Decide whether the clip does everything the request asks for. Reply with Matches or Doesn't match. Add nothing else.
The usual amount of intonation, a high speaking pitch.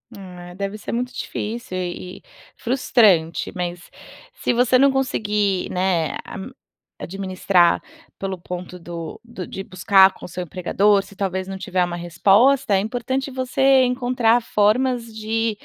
Matches